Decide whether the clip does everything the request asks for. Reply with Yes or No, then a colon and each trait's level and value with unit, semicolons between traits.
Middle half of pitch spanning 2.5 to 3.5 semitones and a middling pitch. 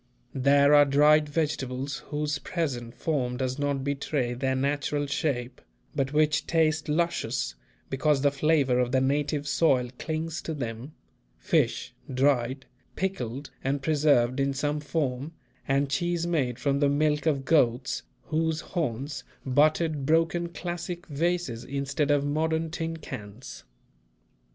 Yes: average, 2.8 semitones; medium, 145 Hz